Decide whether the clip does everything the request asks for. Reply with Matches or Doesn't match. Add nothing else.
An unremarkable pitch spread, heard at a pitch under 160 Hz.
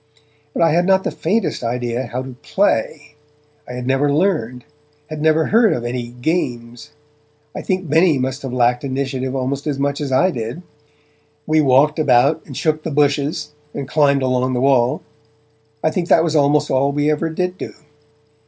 Matches